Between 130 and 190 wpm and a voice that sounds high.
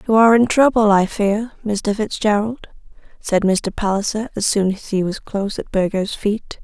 Yes: average, 180 wpm; high, 210 Hz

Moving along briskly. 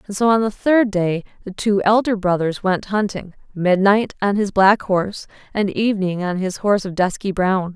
No: average, 185 wpm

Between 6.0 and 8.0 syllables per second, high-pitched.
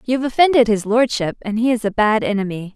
Yes: 6.1 syllables/s; high, 225 Hz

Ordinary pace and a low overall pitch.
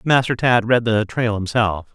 Yes: average, 185 wpm; low, 115 Hz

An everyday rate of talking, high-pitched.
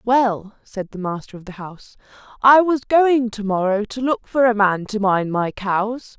Yes: average, 195 wpm; high, 220 Hz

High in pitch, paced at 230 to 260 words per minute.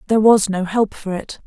Yes: high, 205 Hz; fast, 245 wpm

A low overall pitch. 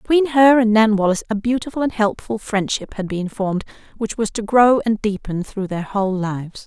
No: high, 215 Hz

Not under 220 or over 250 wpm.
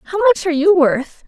Yes: fast, 235 wpm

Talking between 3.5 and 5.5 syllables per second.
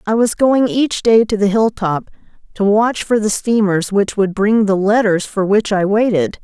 Yes: 4.5 syllables/s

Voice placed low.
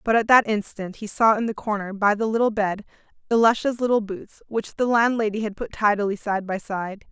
No: high, 215 Hz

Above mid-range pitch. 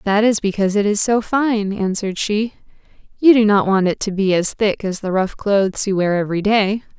Yes: high, 205 Hz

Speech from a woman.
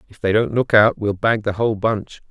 No: male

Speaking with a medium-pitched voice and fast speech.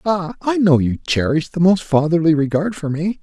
No: medium, 170 Hz; average, 185 wpm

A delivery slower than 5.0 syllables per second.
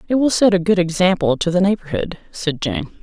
No: 5.6 syllables/s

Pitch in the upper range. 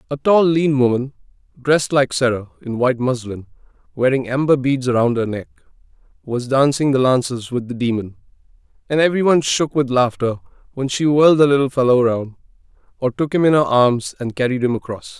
No: low, 130 Hz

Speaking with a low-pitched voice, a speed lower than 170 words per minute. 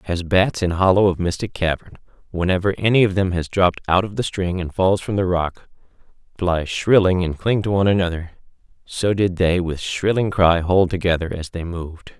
No: very low, 90 Hz; average, 195 wpm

